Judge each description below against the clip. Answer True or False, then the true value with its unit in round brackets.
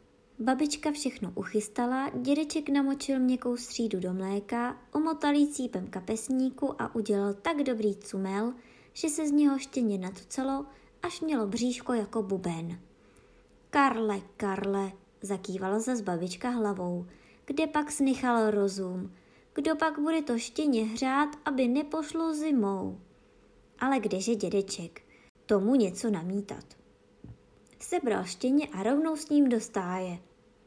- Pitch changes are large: True (5.9 semitones)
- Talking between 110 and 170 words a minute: True (120 wpm)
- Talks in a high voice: True (240 Hz)